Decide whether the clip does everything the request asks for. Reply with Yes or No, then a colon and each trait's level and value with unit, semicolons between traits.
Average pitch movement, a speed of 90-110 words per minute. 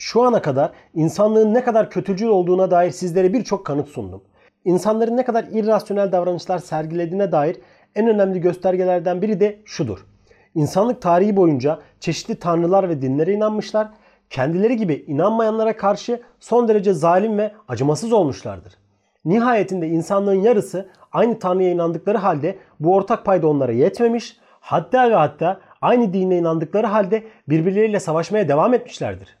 No: average, 4.6 semitones; average, 135 wpm